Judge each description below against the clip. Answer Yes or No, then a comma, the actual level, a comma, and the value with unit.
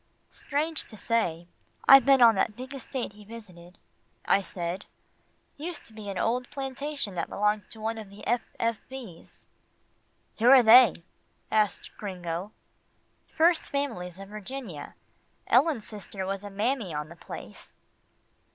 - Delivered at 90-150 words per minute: Yes, average, 145 wpm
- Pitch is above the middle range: Yes, high, 220 Hz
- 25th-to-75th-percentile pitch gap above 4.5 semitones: Yes, average, 5.1 semitones